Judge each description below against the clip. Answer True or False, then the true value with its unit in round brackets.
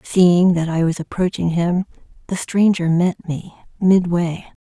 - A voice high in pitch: False (175 Hz)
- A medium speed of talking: True (145 wpm)